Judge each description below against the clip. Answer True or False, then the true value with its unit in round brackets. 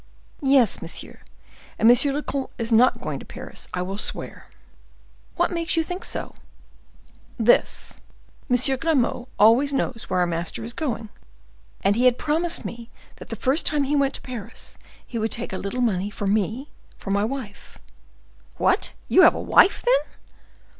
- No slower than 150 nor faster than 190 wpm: True (165 wpm)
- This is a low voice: False (245 Hz)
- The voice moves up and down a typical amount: True (4.6 semitones)